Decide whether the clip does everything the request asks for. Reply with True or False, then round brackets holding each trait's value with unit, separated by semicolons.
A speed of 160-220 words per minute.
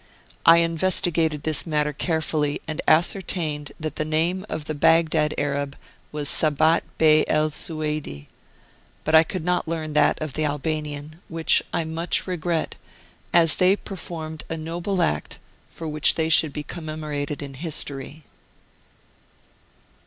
False (140 wpm)